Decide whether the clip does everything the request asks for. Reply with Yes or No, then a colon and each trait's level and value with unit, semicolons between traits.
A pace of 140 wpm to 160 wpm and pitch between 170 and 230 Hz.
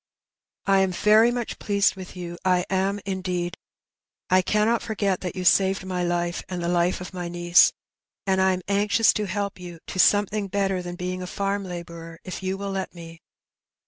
No: average, 190 wpm; medium, 185 Hz